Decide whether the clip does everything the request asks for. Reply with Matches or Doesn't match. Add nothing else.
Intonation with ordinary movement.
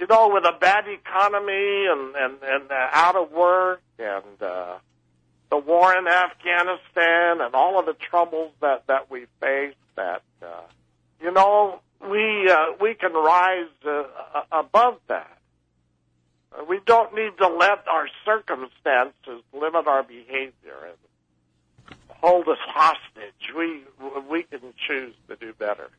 Doesn't match